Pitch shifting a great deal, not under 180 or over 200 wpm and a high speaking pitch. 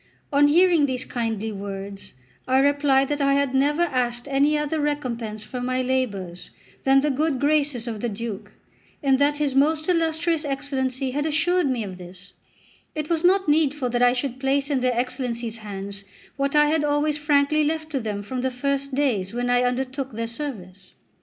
No: average, 3.6 semitones; average, 185 wpm; very high, 270 Hz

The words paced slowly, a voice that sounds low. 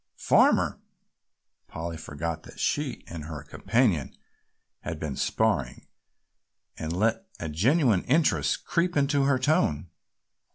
Yes: slow, 115 wpm; very low, 90 Hz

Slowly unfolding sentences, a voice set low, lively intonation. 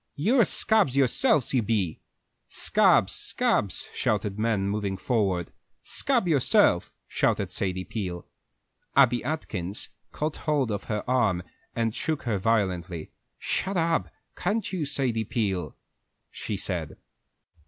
Yes: slow, 120 wpm; low, 115 Hz; wide, 7.3 semitones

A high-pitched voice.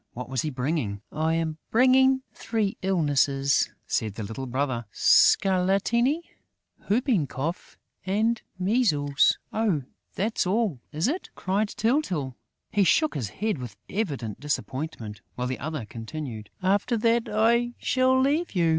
No: medium, 175 Hz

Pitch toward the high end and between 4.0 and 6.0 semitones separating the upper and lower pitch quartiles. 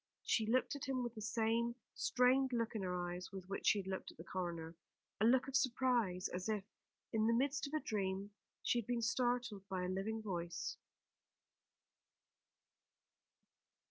Yes: high, 220 Hz; average, 4.6 semitones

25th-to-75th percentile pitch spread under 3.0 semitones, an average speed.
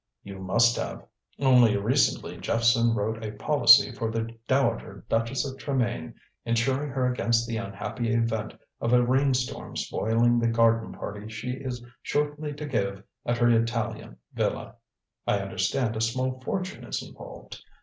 Yes: narrow, 2.5 semitones; average, 150 wpm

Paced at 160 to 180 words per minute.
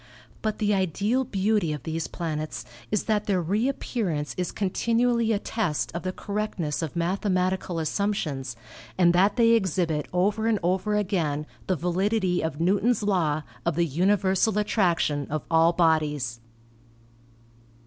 No: average, 145 wpm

